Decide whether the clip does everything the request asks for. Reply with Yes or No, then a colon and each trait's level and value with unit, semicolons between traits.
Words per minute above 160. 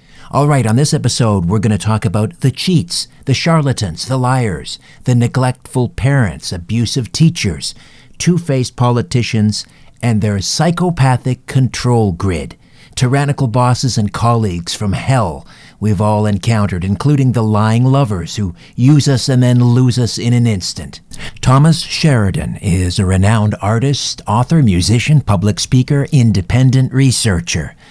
No: slow, 135 wpm